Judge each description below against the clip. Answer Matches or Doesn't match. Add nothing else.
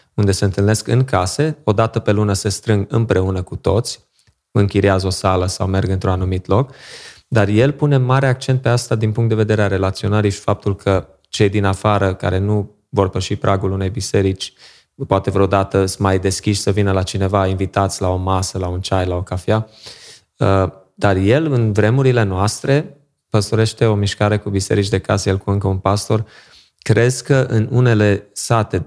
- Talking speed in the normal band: Doesn't match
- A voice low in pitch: Matches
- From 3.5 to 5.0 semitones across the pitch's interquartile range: Doesn't match